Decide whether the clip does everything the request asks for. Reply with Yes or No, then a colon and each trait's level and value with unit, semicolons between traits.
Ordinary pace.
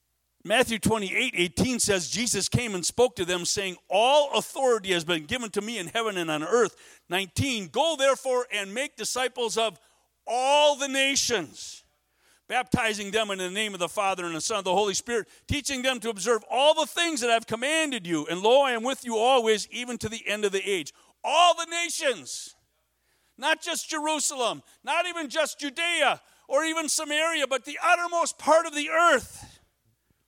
Yes: average, 185 wpm